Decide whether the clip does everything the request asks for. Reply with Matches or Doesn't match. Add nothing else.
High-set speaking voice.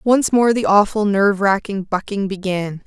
Matches